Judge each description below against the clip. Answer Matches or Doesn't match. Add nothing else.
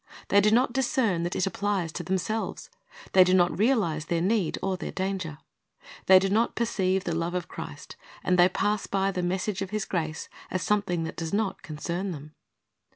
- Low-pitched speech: Doesn't match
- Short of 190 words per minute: Doesn't match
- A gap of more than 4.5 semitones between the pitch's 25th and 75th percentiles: Doesn't match